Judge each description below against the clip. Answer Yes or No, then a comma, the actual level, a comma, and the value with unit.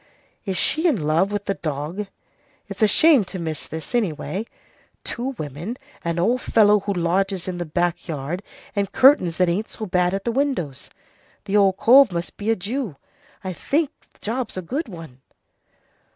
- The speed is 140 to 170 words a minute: No, average, 180 wpm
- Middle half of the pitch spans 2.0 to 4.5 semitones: No, average, 4.9 semitones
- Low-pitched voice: No, high, 195 Hz